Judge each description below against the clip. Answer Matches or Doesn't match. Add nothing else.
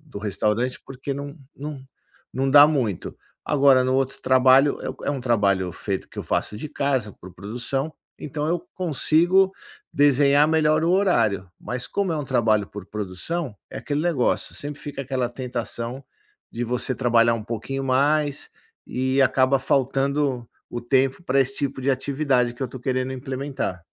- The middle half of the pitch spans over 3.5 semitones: Doesn't match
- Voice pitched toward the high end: Doesn't match